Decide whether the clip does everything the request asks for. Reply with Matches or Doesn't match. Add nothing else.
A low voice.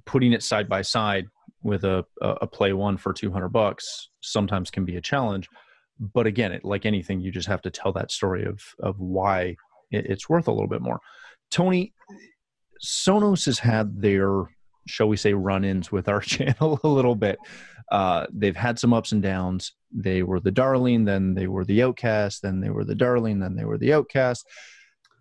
Matches